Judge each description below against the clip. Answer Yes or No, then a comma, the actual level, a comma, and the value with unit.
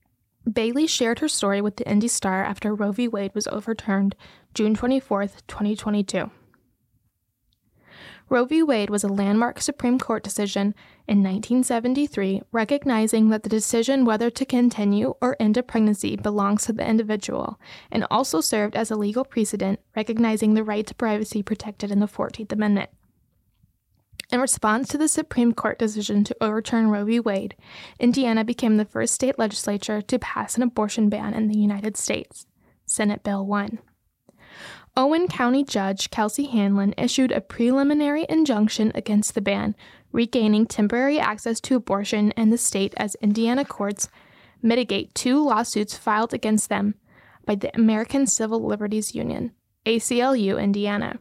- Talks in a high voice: Yes, high, 220 Hz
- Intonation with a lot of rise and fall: No, average, 2.7 semitones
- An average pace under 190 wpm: Yes, average, 150 wpm